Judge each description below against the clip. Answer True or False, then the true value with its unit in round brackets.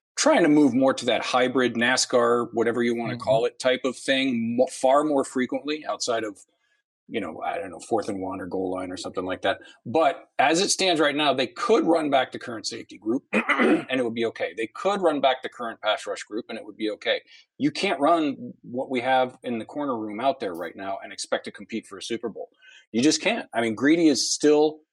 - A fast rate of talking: True (240 wpm)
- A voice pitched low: True (130 Hz)